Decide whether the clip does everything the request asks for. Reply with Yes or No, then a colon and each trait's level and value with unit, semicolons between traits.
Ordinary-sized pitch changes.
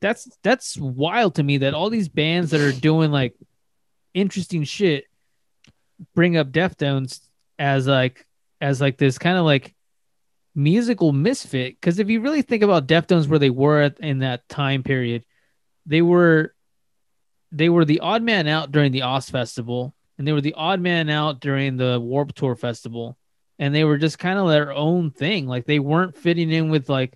Yes: average, 4.1 semitones